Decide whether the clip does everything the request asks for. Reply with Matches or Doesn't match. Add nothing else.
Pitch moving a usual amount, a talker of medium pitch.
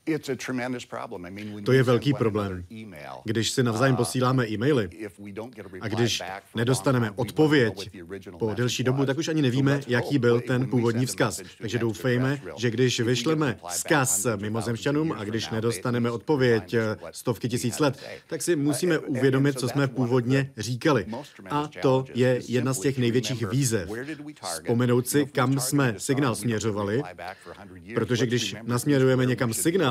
Doesn't match